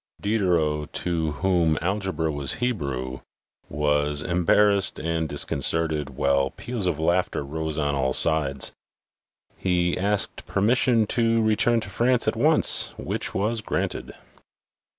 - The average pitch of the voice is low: Yes, very low, 85 Hz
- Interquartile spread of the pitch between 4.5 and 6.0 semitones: Yes, wide, 5.5 semitones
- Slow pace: Yes, slow, 125 wpm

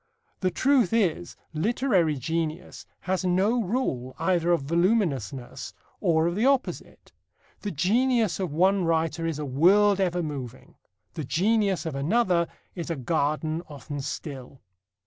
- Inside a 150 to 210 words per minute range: No, slow, 135 wpm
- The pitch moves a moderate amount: Yes, average, 4.7 semitones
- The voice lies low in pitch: No, medium, 170 Hz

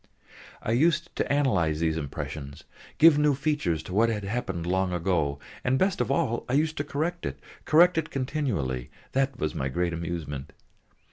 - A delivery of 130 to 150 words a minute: No, average, 175 wpm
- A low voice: Yes, low, 105 Hz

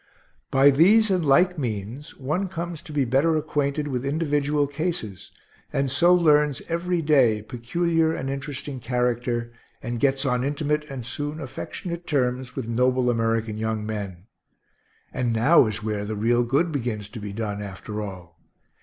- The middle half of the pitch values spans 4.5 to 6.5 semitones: Yes, average, 4.9 semitones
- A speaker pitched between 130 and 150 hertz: Yes, low, 135 Hz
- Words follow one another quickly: No, average, 155 wpm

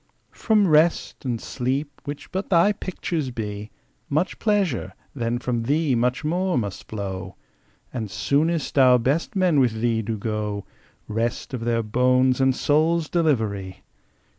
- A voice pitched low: Yes, low, 125 Hz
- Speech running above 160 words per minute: No, average, 140 wpm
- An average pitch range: No, wide, 5.9 semitones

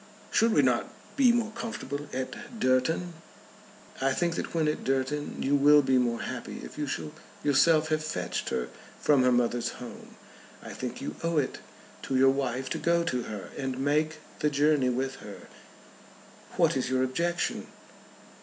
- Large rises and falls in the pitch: No, average, 3.5 semitones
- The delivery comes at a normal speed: Yes, average, 170 wpm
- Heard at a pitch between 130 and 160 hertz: Yes, medium, 140 Hz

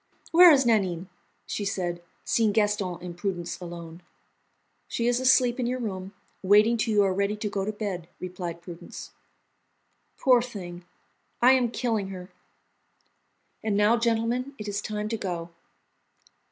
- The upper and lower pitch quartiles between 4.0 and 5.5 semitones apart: Yes, average, 4.3 semitones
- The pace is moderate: Yes, average, 150 wpm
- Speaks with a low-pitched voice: No, high, 205 Hz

